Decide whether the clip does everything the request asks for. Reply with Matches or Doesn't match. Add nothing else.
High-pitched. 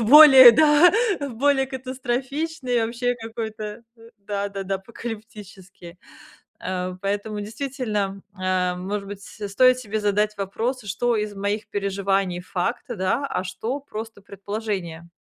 Matches